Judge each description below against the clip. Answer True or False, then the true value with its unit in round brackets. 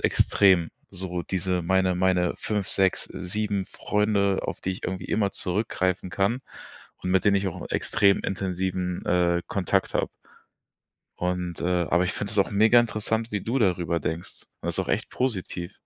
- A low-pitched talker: True (95 Hz)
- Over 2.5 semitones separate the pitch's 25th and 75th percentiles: False (2.2 semitones)